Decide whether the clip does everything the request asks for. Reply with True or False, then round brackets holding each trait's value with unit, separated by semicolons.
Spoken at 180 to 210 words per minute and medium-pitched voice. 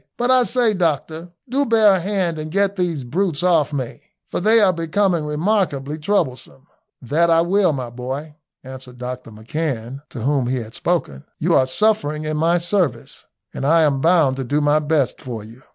True (185 wpm; 155 Hz)